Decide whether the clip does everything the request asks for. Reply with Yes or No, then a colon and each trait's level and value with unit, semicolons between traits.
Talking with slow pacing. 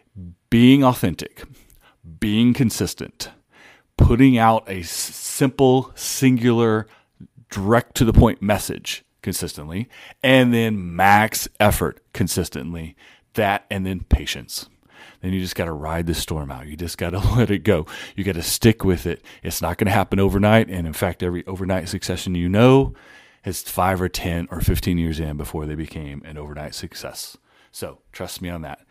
No: average, 165 wpm